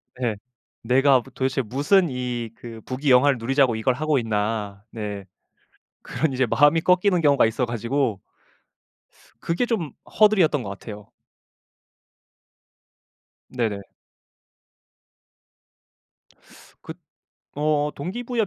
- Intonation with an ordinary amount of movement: Yes, average, 4.8 semitones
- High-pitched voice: No, low, 130 Hz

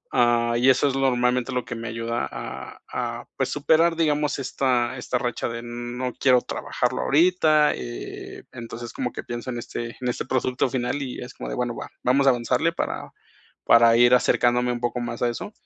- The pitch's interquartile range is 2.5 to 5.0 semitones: No, narrow, 1.8 semitones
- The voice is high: No, low, 125 Hz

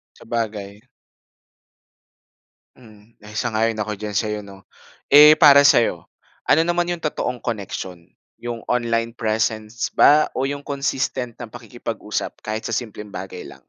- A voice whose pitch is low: Yes, low, 115 Hz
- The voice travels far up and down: No, average, 3.3 semitones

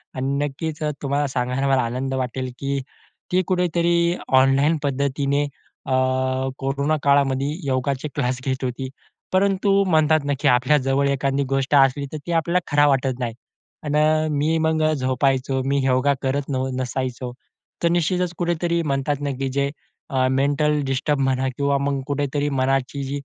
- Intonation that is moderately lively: No, narrow, 2.0 semitones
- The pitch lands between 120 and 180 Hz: Yes, medium, 140 Hz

